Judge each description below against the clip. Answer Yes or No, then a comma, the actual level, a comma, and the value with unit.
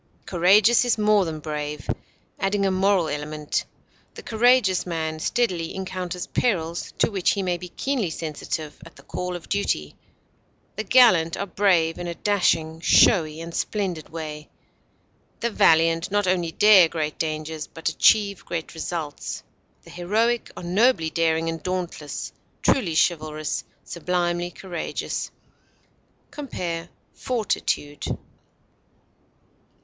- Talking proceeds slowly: Yes, slow, 125 wpm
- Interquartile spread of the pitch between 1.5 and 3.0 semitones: No, average, 3.7 semitones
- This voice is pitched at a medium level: Yes, medium, 175 Hz